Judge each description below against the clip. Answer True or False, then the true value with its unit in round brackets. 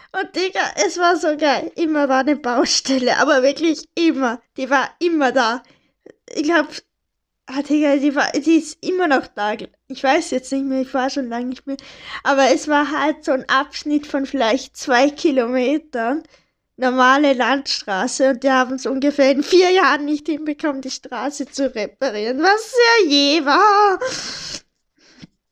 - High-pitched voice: True (280 Hz)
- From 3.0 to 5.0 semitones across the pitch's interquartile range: True (3.3 semitones)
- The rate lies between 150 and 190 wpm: True (165 wpm)